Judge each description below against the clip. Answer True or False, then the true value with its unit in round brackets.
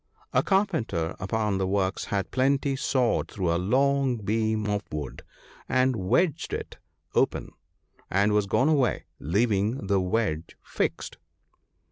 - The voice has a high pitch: False (105 Hz)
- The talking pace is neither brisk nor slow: False (130 wpm)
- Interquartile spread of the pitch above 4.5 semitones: True (5.2 semitones)